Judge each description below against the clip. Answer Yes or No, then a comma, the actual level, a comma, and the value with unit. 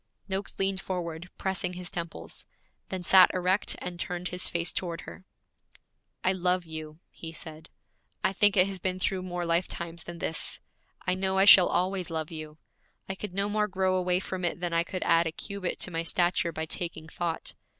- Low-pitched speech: No, medium, 180 Hz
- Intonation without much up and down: Yes, narrow, 2.0 semitones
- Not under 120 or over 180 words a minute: No, average, 190 wpm